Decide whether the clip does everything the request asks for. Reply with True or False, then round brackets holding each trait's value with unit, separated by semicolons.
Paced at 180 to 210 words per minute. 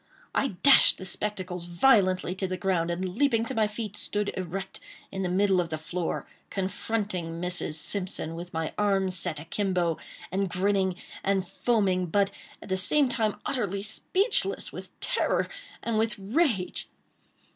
False (155 wpm)